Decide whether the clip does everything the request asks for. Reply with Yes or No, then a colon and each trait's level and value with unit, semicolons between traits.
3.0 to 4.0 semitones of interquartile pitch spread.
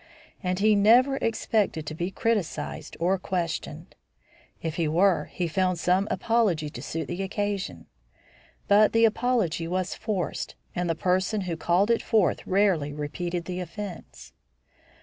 Yes: average, 3.7 semitones